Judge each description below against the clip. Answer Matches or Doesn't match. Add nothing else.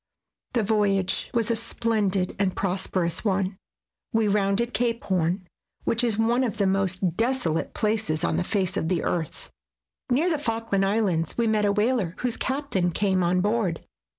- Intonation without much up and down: Doesn't match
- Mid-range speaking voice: Doesn't match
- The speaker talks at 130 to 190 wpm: Matches